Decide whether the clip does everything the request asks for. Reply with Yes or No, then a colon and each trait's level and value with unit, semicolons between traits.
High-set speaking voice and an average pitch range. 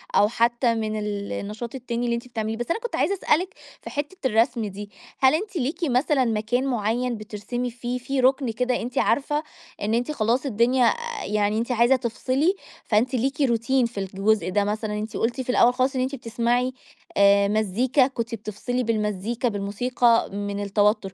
Yes: high, 235 Hz; average, 3.2 semitones